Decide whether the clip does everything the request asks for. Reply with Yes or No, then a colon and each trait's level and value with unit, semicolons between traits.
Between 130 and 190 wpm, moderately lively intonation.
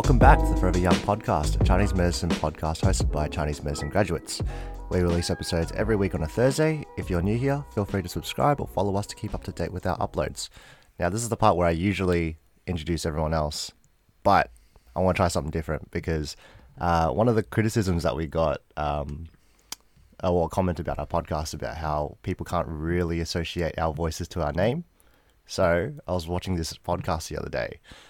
No: fast, 205 wpm; average, 3.0 semitones